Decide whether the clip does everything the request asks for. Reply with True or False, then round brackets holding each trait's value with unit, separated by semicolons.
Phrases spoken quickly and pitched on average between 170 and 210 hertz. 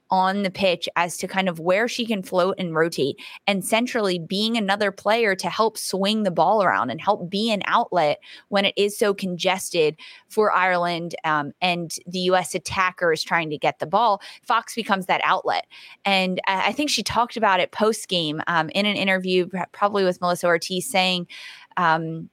False (190 wpm; 190 Hz)